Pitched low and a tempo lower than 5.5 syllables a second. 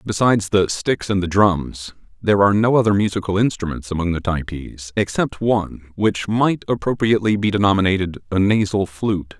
No: low, 100 Hz; 5.6 syllables/s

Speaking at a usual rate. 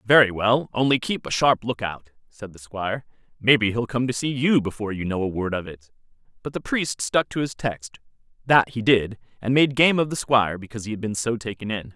No: fast, 225 wpm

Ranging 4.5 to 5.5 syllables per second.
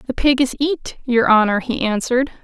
Yes: 5.3 syllables/s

